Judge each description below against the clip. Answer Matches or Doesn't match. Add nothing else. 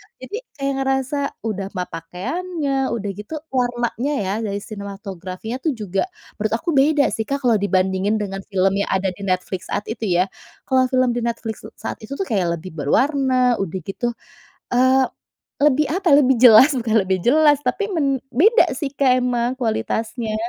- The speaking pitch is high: Matches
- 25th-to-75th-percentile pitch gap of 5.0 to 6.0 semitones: Matches